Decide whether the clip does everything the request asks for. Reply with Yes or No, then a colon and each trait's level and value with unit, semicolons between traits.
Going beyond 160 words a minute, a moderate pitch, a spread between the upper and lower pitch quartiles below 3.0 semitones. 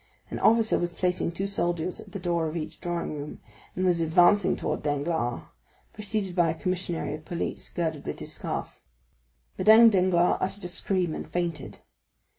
Yes: average, 170 wpm; medium, 175 Hz; narrow, 2.5 semitones